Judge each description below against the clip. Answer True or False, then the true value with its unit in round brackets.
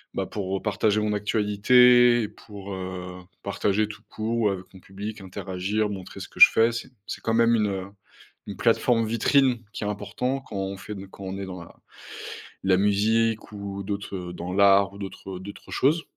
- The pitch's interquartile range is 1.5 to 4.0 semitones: True (2.5 semitones)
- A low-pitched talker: True (100 Hz)